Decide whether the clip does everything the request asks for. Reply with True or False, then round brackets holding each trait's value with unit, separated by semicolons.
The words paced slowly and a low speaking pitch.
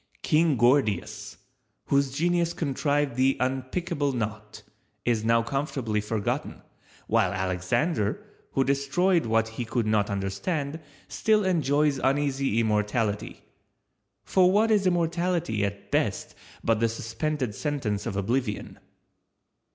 True (110 wpm; 130 Hz)